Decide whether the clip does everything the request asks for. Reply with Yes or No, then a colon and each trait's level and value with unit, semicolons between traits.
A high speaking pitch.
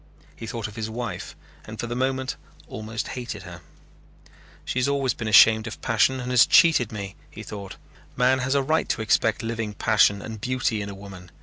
No: low, 115 Hz